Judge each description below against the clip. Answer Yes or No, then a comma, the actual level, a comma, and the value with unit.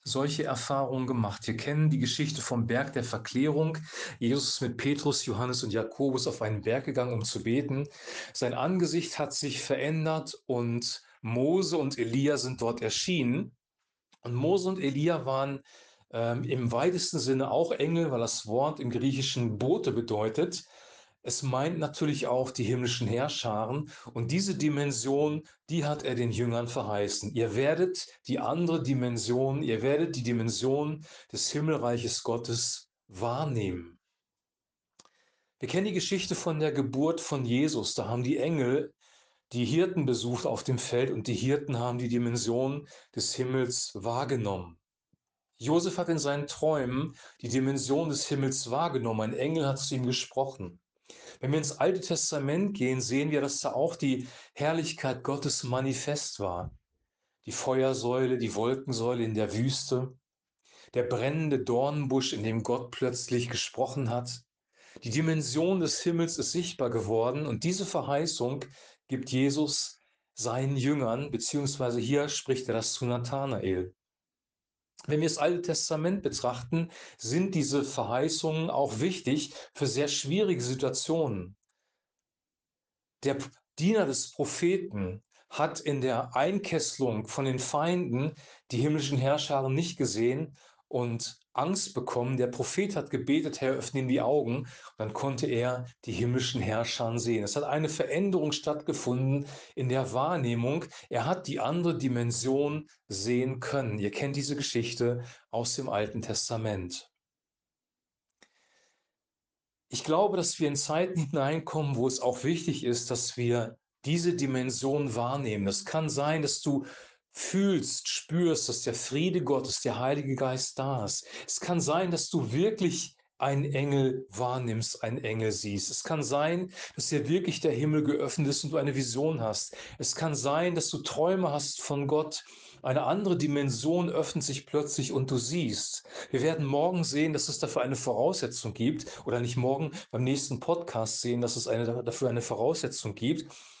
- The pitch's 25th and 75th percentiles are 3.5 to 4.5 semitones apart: Yes, average, 4.0 semitones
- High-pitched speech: No, low, 135 Hz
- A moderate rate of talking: Yes, average, 150 wpm